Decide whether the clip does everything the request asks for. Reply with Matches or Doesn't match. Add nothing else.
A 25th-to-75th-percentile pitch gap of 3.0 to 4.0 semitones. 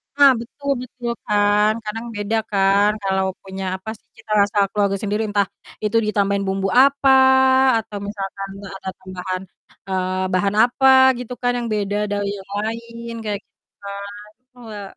Doesn't match